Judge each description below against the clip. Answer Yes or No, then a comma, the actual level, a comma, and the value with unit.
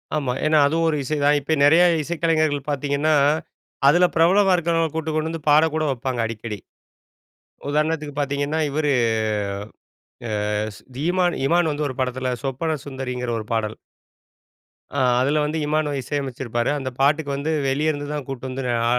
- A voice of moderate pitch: Yes, medium, 145 Hz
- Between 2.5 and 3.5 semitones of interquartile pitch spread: Yes, average, 2.9 semitones